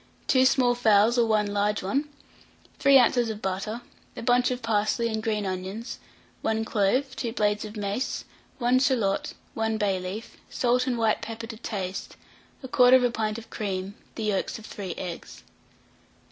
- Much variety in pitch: No, average, 3.0 semitones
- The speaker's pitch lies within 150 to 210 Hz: No, high, 220 Hz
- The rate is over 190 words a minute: No, average, 160 wpm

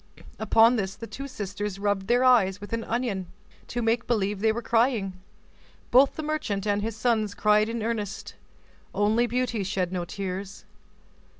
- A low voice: No, high, 215 Hz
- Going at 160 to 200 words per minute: Yes, average, 165 wpm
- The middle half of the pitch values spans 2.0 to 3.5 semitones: Yes, average, 2.9 semitones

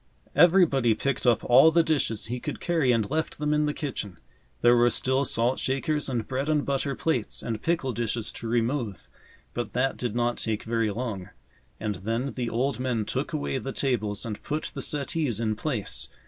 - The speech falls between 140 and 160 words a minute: No, average, 190 wpm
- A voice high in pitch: No, low, 125 Hz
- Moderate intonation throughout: Yes, average, 3.8 semitones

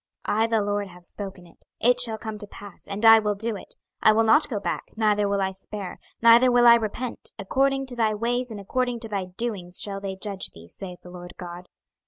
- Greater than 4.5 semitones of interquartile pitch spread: No, average, 3.1 semitones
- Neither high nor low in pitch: No, high, 210 Hz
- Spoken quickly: Yes, fast, 235 wpm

